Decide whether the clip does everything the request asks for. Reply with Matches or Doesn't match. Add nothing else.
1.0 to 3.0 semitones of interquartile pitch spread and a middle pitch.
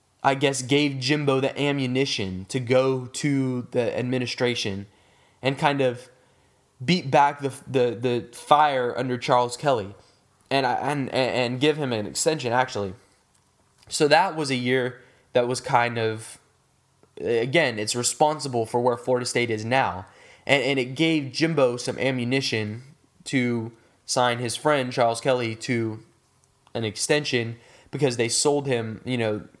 Doesn't match